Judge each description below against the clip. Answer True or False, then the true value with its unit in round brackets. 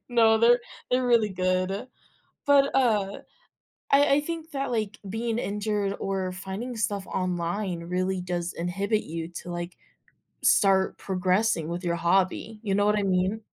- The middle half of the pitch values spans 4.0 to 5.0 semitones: False (3.5 semitones)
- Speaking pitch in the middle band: False (195 Hz)